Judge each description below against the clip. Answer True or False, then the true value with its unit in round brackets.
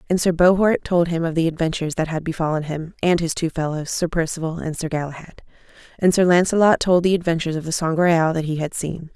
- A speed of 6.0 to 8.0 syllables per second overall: True (6.1 syllables/s)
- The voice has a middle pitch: True (165 Hz)